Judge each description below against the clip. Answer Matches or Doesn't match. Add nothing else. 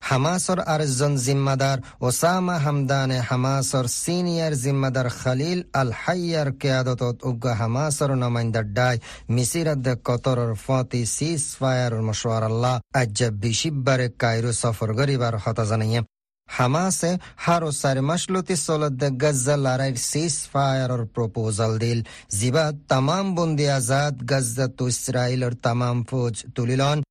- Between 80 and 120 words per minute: Doesn't match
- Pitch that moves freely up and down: Doesn't match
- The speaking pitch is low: Matches